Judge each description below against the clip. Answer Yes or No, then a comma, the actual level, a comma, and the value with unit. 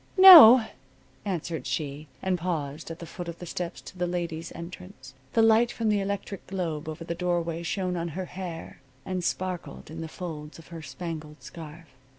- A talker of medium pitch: Yes, medium, 170 Hz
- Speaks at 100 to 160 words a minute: No, average, 180 wpm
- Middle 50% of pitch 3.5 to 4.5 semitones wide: No, narrow, 2.5 semitones